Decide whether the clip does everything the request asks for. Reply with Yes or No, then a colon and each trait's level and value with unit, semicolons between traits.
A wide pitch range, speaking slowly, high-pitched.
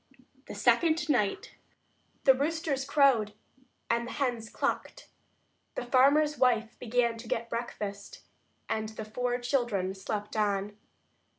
No: average, 3.9 semitones; slow, 120 wpm; high, 235 Hz